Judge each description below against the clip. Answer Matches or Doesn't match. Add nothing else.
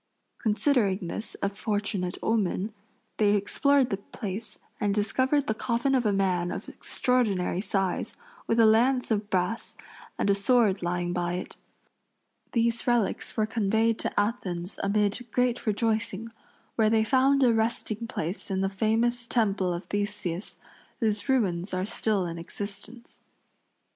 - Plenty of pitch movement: Doesn't match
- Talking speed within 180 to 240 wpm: Doesn't match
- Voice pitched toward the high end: Matches